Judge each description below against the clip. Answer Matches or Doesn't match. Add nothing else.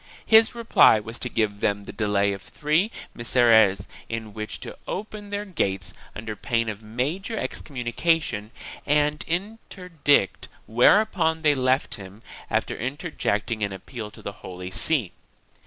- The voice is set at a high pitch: Doesn't match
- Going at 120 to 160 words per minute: Matches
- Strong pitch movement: Matches